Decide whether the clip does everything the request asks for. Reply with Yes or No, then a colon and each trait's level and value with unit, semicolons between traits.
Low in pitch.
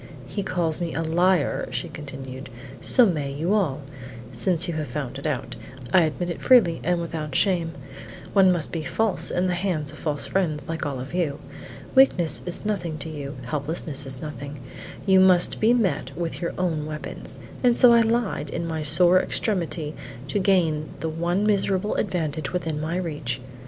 No: medium, 165 Hz